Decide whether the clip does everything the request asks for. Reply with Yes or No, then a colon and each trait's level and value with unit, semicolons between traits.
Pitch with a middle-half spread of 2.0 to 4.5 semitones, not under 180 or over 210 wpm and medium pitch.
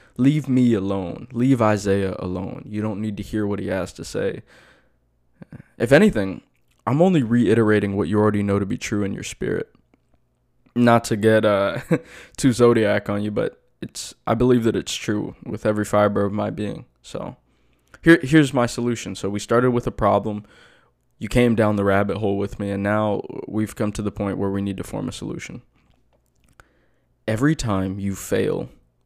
No: average, 3.2 semitones; average, 185 wpm; low, 105 Hz